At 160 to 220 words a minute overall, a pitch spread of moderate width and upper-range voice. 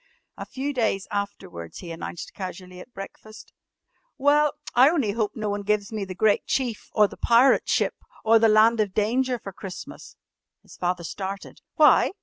Yes: average, 170 wpm; average, 3.3 semitones; high, 210 Hz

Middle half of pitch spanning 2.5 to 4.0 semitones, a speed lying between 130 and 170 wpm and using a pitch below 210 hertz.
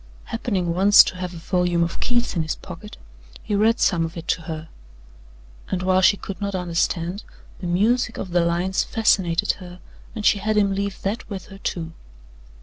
No: average, 3.0 semitones; average, 190 wpm; medium, 185 Hz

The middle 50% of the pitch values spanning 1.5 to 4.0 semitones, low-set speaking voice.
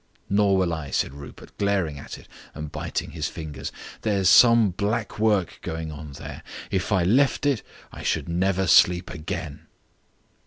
No: average, 4.6 semitones; very low, 90 Hz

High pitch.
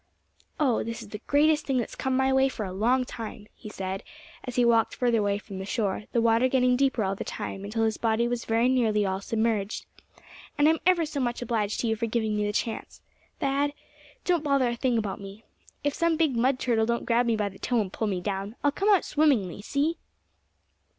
Yes: high, 235 Hz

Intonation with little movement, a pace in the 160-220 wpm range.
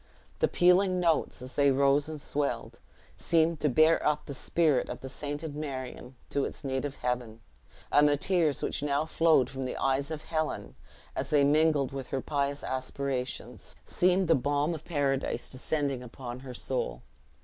No: average, 3.0 semitones; average, 170 wpm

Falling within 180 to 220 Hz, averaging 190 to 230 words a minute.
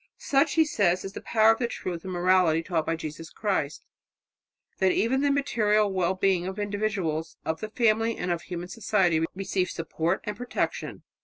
No: high, 190 Hz; average, 180 wpm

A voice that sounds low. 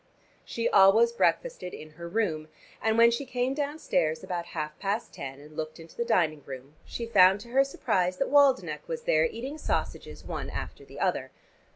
No: high, 205 Hz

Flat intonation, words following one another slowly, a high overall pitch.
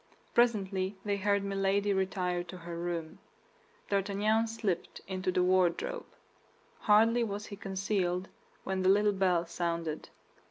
Yes: narrow, 2.2 semitones; slow, 125 wpm; high, 195 Hz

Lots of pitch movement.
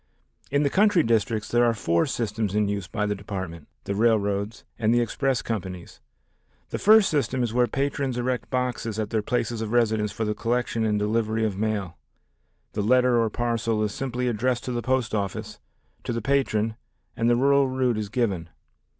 No: average, 3.0 semitones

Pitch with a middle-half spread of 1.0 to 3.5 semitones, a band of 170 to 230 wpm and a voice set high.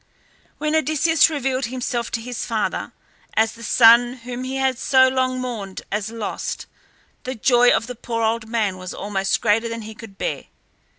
Yes: average, 2.7 semitones; average, 175 wpm; high, 235 Hz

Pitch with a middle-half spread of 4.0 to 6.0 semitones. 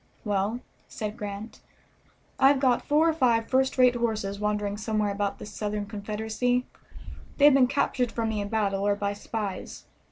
No: average, 3.4 semitones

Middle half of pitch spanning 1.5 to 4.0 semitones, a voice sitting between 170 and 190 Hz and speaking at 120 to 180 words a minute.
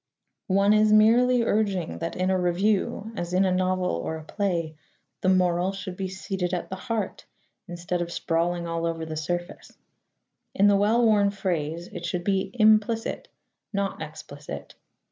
Yes: average, 2.9 semitones; medium, 185 Hz; average, 165 wpm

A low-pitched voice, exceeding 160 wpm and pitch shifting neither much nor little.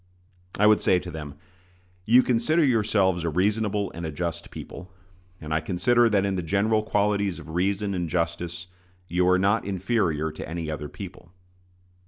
Yes: very low, 95 Hz; average, 170 wpm; average, 3.7 semitones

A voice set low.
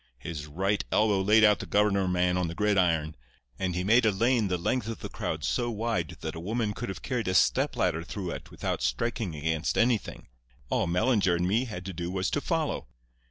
Yes: very low, 95 Hz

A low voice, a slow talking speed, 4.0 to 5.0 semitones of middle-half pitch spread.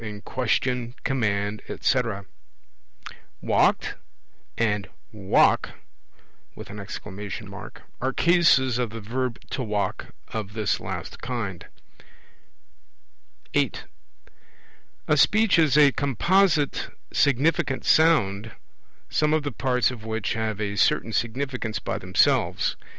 Yes: low, 120 Hz; slow, 100 wpm; average, 4.7 semitones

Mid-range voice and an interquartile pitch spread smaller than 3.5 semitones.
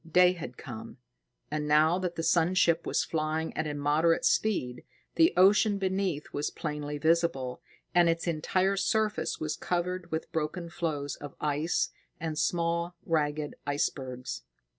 Yes: medium, 160 Hz; average, 3.1 semitones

